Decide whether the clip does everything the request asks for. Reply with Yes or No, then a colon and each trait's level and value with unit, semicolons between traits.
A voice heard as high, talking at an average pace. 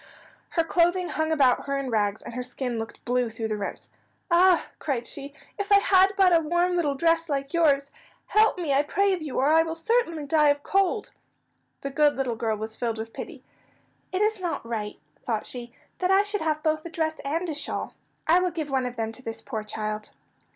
No: very high, 300 Hz; fast, 220 wpm